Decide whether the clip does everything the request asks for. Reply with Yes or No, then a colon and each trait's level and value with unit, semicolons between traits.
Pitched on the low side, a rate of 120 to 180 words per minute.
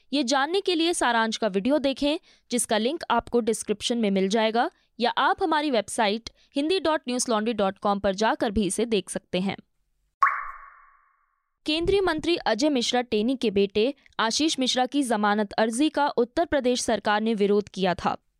No: high, 245 Hz; average, 155 wpm